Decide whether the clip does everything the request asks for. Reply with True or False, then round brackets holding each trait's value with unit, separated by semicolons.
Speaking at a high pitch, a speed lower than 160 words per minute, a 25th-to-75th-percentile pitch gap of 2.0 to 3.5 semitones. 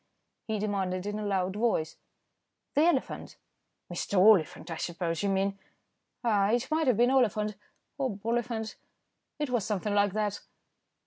True (210 Hz; 145 wpm; 3.2 semitones)